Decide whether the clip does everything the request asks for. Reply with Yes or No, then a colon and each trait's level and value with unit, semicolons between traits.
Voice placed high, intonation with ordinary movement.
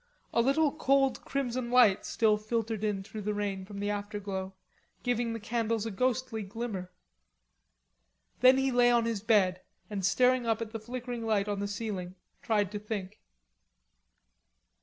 Yes: high, 220 Hz; average, 3.0 semitones